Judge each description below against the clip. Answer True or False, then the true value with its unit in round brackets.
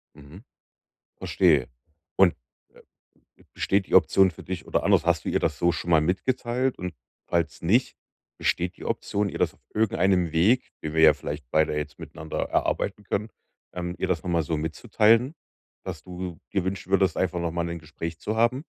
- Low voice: True (90 Hz)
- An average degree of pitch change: True (3.5 semitones)